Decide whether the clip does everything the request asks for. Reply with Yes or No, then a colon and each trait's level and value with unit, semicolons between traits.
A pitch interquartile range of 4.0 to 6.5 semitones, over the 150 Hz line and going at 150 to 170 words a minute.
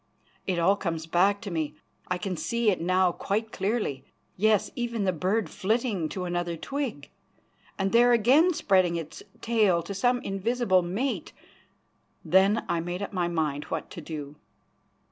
Yes: average, 4.4 semitones; high, 190 Hz; average, 160 wpm